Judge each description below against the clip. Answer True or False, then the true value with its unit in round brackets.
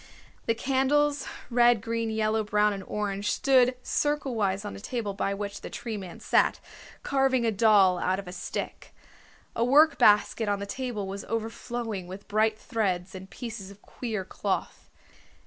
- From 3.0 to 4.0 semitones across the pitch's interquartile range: True (3.3 semitones)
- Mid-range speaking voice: False (215 Hz)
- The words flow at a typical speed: True (160 wpm)